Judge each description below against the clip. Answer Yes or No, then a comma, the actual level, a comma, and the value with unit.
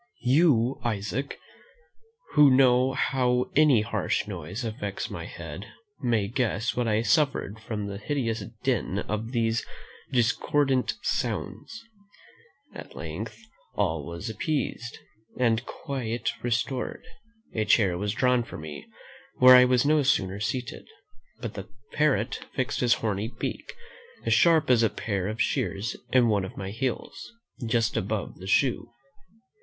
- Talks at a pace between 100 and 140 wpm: Yes, slow, 135 wpm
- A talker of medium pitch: No, low, 115 Hz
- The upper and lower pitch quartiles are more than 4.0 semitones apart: No, average, 3.7 semitones